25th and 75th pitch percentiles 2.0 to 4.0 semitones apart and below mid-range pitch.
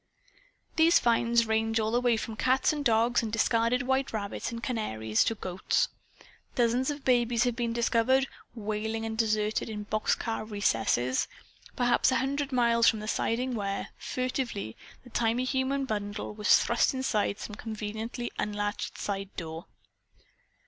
No: average, 2.7 semitones; high, 230 Hz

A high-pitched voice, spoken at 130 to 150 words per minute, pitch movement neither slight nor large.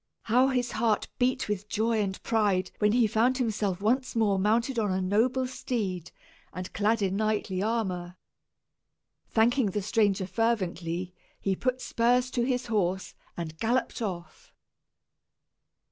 Yes: high, 215 Hz; average, 140 wpm; average, 3.9 semitones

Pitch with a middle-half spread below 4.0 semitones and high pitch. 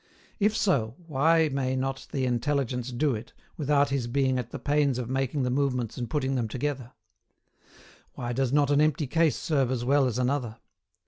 No: narrow, 2.5 semitones; low, 135 Hz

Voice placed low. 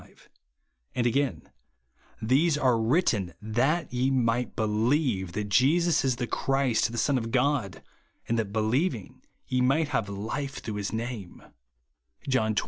Yes: low, 120 Hz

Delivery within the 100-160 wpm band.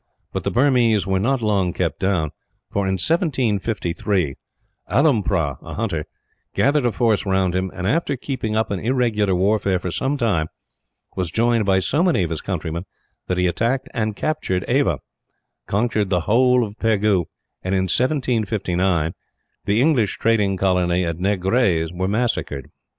Yes: average, 155 wpm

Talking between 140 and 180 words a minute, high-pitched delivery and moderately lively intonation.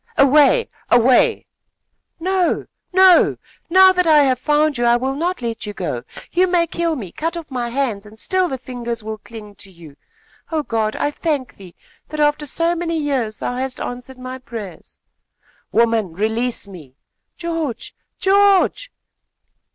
No: average, 160 wpm; very high, 260 Hz; wide, 6.6 semitones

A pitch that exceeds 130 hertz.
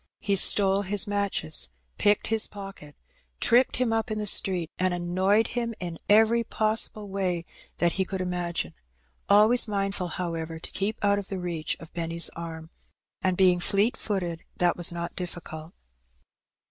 Yes: high, 190 Hz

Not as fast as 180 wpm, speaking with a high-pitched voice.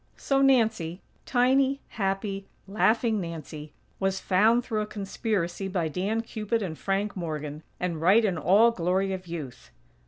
Yes: average, 145 wpm; high, 195 Hz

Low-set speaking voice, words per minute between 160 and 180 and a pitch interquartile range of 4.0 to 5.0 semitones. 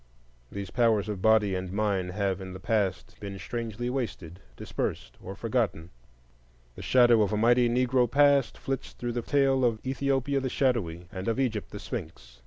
Yes: low, 115 Hz; average, 175 wpm; average, 4.4 semitones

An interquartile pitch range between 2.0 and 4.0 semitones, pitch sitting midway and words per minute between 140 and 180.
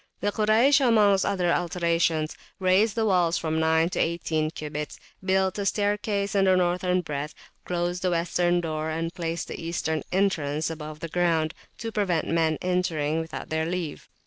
Yes: average, 3.0 semitones; medium, 175 Hz; average, 170 wpm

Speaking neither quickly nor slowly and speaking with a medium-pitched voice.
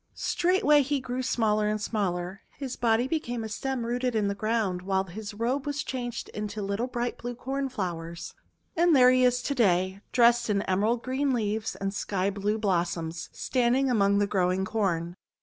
No: average, 175 wpm; high, 220 Hz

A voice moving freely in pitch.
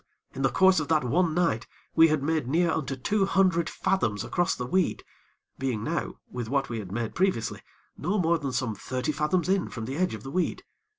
Yes: wide, 5.9 semitones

